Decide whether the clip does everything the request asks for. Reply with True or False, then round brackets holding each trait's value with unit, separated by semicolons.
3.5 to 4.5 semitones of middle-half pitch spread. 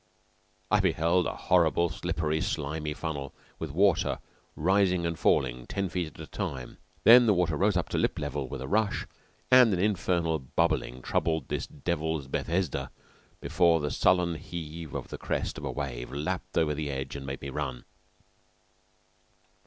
True (4.0 semitones)